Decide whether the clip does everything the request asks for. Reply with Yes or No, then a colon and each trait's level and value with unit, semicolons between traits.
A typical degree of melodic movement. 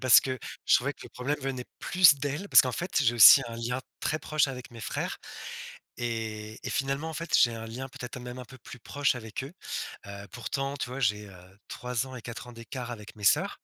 Yes: average, 3.1 semitones